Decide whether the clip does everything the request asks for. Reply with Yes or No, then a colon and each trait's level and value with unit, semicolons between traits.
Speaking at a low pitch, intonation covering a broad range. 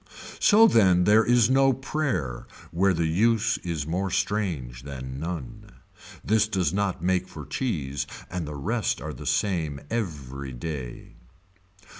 Yes: very low, 90 Hz; wide, 6.9 semitones